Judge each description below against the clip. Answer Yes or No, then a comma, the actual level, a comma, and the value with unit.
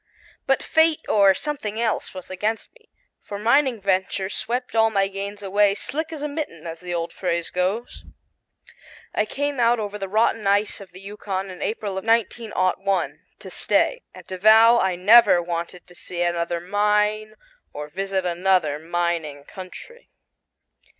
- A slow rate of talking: No, average, 160 wpm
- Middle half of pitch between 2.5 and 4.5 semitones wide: Yes, average, 3.7 semitones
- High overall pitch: Yes, high, 200 Hz